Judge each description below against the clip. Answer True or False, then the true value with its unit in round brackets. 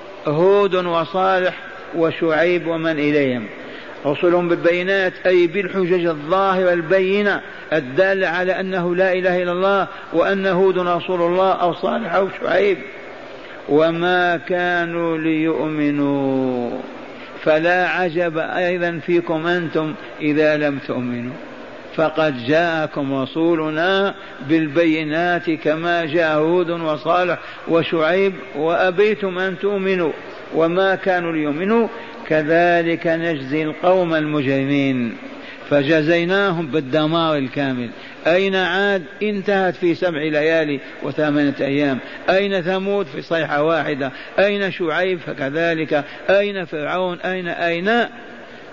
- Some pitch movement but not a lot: True (3.2 semitones)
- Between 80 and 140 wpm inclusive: True (95 wpm)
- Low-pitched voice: False (170 Hz)